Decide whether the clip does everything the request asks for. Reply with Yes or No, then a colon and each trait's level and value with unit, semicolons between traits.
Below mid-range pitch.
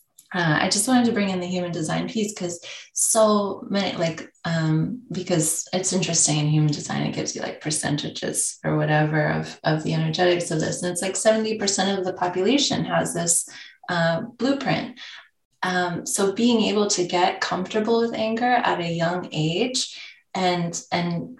No: medium, 180 Hz